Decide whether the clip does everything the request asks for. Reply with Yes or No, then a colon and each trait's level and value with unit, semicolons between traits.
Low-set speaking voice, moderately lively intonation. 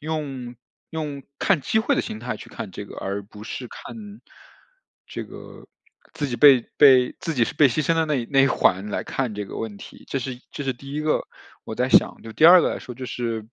Yes: low, 130 Hz; average, 4.4 semitones